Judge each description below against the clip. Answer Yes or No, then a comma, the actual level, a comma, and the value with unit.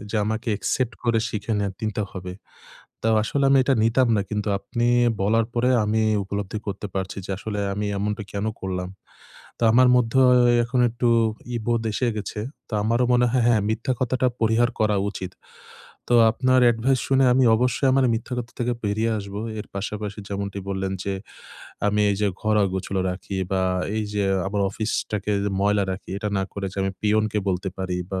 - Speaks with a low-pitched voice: Yes, low, 105 Hz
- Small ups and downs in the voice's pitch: No, average, 3.0 semitones